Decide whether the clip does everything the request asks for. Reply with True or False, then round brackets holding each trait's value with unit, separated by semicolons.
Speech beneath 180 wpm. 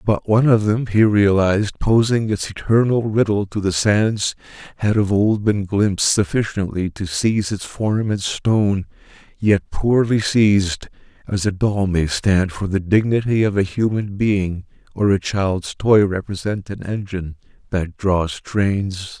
True (155 wpm)